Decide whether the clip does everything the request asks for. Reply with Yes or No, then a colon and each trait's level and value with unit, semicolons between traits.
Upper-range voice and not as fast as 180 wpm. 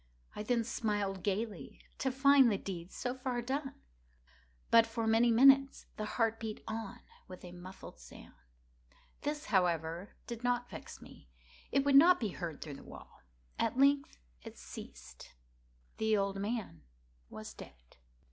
Yes: high, 225 Hz; average, 150 wpm